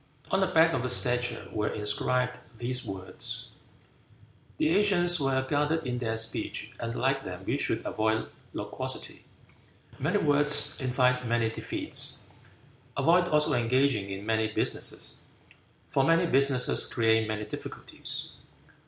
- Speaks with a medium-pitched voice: No, low, 125 Hz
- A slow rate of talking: Yes, slow, 130 wpm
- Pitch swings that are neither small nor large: Yes, average, 4.5 semitones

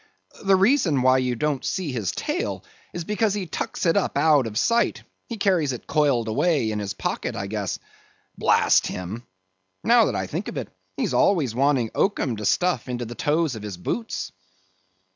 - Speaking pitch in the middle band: Yes, medium, 145 Hz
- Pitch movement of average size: No, wide, 8.5 semitones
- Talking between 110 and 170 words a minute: No, average, 185 wpm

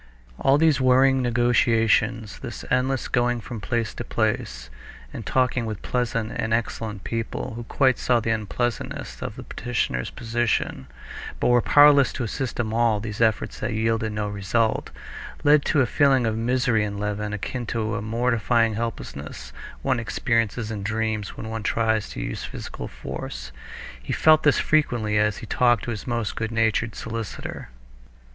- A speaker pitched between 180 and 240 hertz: No, low, 115 Hz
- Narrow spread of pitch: Yes, narrow, 2.2 semitones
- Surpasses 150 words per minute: Yes, average, 160 wpm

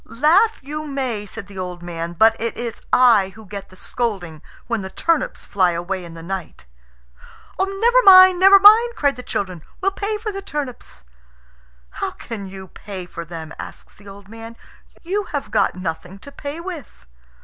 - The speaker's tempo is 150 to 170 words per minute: No, average, 180 wpm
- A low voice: No, high, 225 Hz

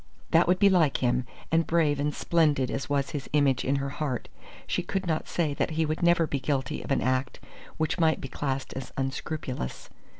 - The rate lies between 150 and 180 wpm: No, fast, 205 wpm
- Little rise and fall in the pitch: No, average, 3.3 semitones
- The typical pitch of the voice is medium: Yes, medium, 145 Hz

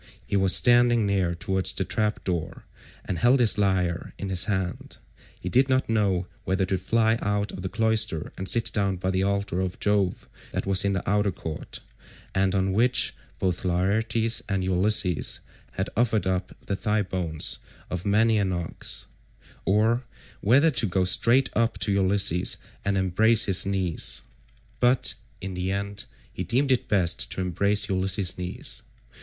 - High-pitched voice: No, low, 100 Hz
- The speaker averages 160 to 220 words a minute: Yes, average, 165 wpm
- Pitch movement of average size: Yes, average, 3.0 semitones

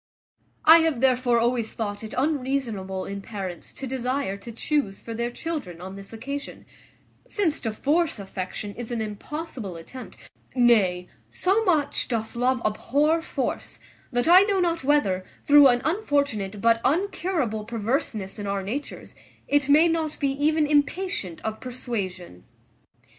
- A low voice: No, high, 245 Hz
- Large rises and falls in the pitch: Yes, wide, 6.1 semitones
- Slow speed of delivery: No, average, 145 wpm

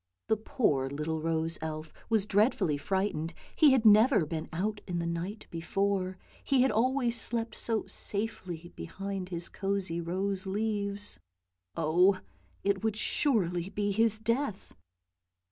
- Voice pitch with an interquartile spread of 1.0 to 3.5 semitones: No, average, 4.4 semitones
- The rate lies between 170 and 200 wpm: No, average, 140 wpm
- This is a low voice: No, high, 195 Hz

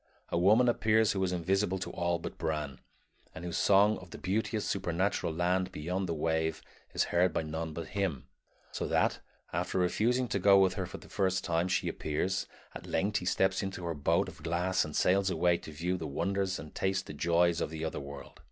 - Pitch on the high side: No, very low, 90 Hz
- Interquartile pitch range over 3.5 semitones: No, average, 2.9 semitones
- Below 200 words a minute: No, fast, 205 wpm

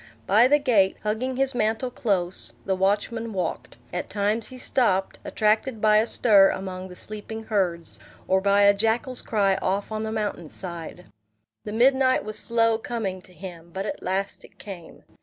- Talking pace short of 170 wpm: No, average, 175 wpm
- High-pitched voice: Yes, high, 210 Hz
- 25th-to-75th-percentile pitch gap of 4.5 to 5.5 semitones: No, average, 3.1 semitones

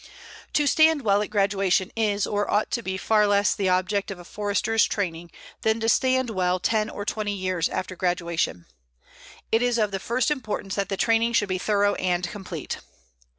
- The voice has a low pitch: No, high, 205 Hz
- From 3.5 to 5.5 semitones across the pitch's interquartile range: No, average, 3.0 semitones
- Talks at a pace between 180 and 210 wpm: Yes, average, 190 wpm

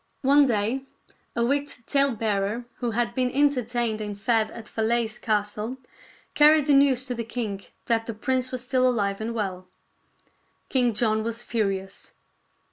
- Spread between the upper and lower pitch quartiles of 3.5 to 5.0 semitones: No, average, 3.0 semitones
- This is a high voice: Yes, high, 235 Hz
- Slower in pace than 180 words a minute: Yes, average, 150 wpm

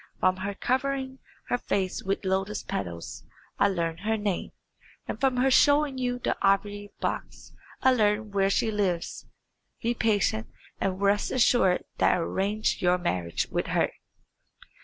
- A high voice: Yes, high, 205 Hz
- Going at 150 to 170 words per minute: Yes, average, 155 wpm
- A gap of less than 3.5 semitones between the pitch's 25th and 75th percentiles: No, average, 4.3 semitones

